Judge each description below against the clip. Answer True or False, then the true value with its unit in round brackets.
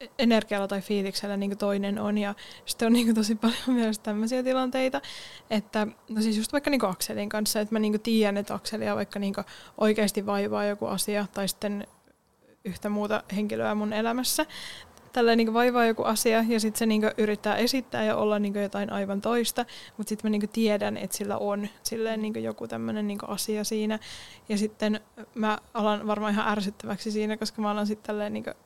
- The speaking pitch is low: False (215 Hz)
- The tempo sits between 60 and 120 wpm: False (155 wpm)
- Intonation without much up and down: True (1.4 semitones)